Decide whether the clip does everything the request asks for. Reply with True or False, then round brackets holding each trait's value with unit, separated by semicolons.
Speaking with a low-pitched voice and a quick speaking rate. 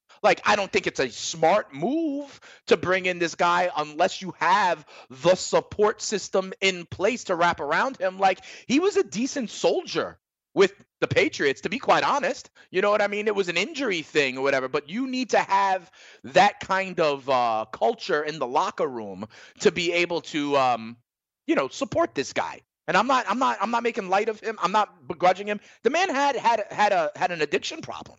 False (195 Hz; 210 wpm)